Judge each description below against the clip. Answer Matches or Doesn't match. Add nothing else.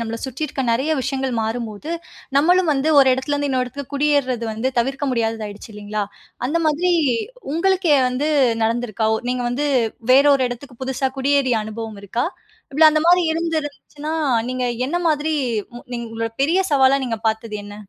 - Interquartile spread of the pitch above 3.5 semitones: Matches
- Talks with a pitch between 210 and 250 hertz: Doesn't match